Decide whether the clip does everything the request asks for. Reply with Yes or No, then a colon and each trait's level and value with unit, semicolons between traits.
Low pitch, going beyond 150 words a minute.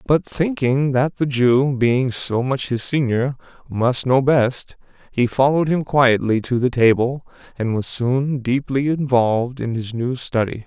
Yes: low, 130 Hz; average, 165 wpm